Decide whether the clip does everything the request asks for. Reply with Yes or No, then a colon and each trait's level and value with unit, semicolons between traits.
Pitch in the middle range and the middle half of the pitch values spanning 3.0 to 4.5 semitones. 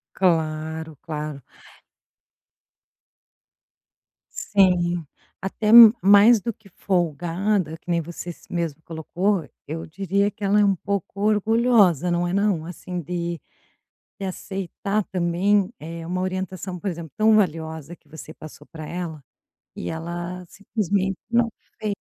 Yes: medium, 180 Hz; average, 3.5 semitones